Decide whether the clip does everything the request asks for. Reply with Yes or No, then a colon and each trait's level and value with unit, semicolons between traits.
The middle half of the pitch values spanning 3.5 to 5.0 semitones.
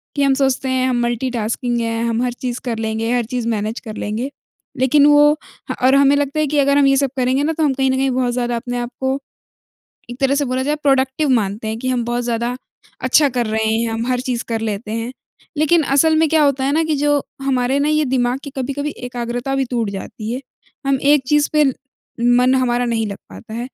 No: average, 2.8 semitones